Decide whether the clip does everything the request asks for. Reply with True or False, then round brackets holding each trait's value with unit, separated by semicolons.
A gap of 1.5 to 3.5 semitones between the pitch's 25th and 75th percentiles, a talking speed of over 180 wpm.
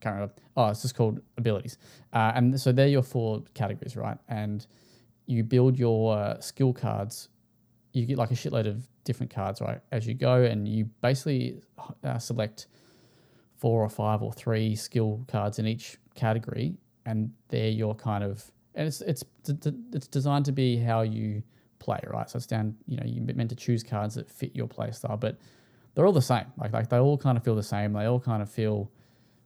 True (2.5 semitones; 200 wpm)